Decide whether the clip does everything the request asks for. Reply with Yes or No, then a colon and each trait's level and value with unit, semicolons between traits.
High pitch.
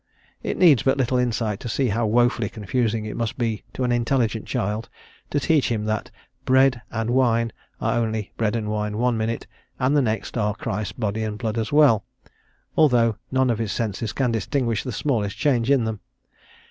No: low, 115 Hz